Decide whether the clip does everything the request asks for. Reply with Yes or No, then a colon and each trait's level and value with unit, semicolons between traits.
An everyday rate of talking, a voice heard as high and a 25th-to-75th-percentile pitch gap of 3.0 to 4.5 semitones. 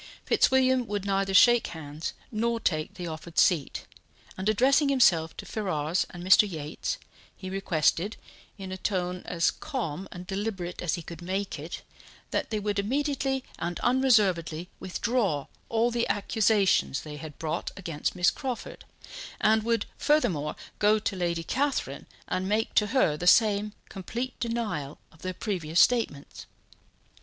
No: average, 150 wpm; high, 195 Hz; average, 5.2 semitones